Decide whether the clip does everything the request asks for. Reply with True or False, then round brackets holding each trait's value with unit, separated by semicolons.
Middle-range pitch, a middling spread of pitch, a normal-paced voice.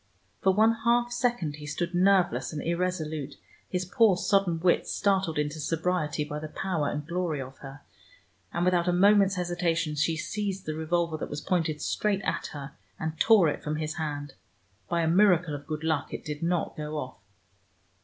True (165 Hz; 3.4 semitones; 185 wpm)